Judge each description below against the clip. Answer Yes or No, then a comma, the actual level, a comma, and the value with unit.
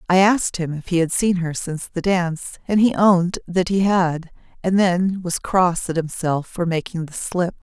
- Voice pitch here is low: No, medium, 175 Hz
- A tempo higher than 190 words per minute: Yes, average, 200 wpm